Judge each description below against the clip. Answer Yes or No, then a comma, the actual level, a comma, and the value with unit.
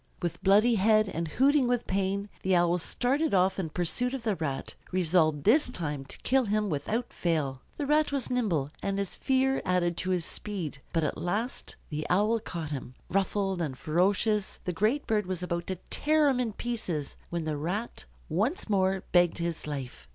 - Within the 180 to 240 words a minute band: Yes, average, 190 wpm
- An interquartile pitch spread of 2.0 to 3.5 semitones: No, average, 5.3 semitones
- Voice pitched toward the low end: No, high, 190 Hz